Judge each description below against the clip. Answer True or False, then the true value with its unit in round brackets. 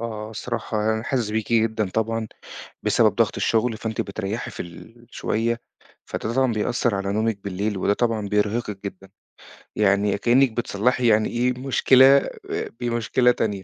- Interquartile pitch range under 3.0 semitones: True (2.4 semitones)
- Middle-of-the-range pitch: False (110 Hz)